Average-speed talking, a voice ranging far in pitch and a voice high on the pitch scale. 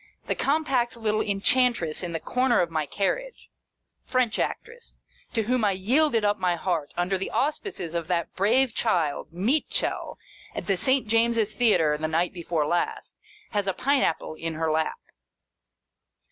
Yes: average, 165 wpm; wide, 6.5 semitones; high, 205 Hz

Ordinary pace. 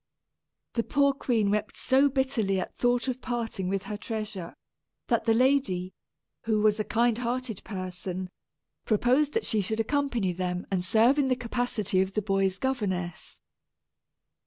Yes: average, 150 wpm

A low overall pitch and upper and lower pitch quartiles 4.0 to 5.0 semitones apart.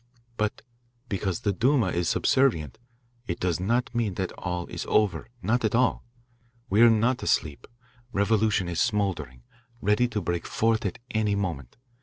Yes: low, 100 Hz; average, 4.3 semitones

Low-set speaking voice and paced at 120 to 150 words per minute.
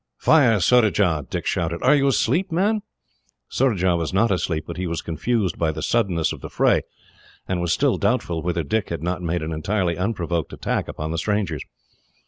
No: very low, 90 Hz; average, 185 wpm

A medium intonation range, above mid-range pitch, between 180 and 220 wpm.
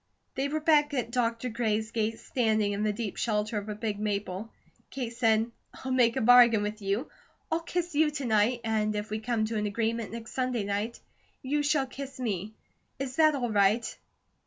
Yes: average, 3.3 semitones; high, 230 Hz; average, 195 wpm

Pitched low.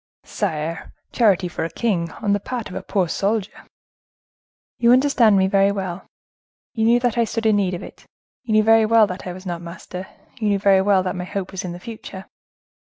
No: high, 200 Hz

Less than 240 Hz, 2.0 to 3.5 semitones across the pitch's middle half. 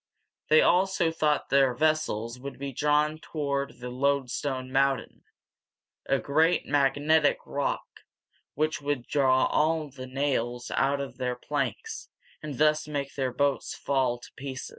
Yes: medium, 140 Hz; narrow, 2.5 semitones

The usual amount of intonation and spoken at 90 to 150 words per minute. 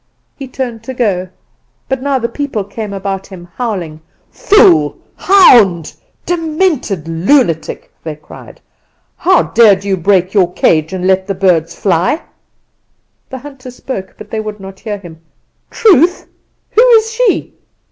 No: wide, 6.8 semitones; average, 140 wpm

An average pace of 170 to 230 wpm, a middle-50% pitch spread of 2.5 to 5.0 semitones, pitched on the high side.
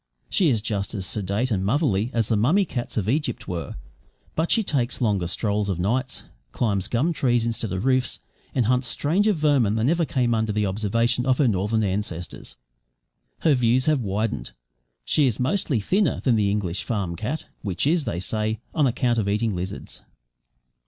No: average, 180 wpm; average, 4.5 semitones; low, 115 Hz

